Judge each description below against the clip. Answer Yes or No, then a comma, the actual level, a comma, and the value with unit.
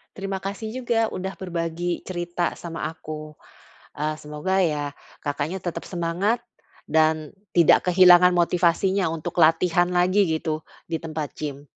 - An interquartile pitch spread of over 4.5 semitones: No, average, 2.8 semitones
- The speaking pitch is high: No, medium, 170 Hz